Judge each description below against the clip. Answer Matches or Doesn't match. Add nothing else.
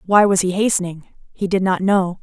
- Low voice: Doesn't match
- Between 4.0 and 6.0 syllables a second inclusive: Matches